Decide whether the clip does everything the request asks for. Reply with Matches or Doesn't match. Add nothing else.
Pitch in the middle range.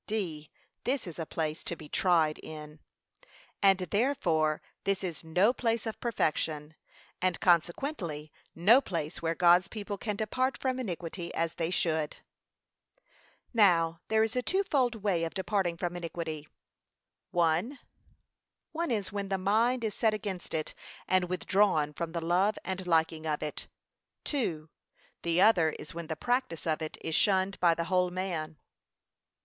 Matches